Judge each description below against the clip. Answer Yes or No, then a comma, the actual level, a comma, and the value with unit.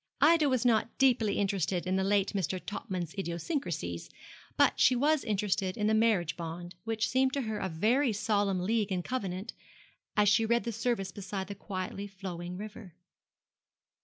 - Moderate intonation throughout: Yes, average, 3.6 semitones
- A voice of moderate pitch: No, high, 205 Hz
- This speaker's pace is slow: No, average, 165 wpm